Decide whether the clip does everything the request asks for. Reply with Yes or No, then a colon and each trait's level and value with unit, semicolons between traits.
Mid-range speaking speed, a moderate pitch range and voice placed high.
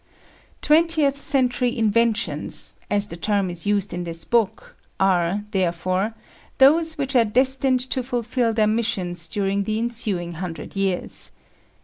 No: slow, 130 wpm; average, 5.0 semitones; high, 215 Hz